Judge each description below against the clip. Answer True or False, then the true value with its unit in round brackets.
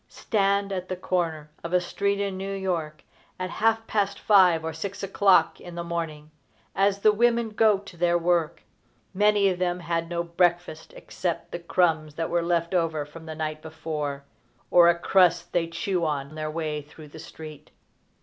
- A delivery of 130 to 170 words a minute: False (180 wpm)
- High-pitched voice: False (175 Hz)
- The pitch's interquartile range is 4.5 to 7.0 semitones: False (3.2 semitones)